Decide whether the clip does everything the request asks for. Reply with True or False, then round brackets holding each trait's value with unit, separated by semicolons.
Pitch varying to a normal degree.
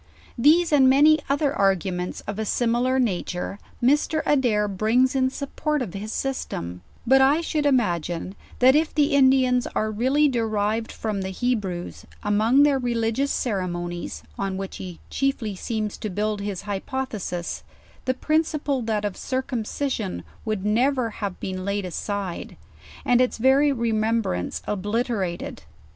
True (5.0 semitones)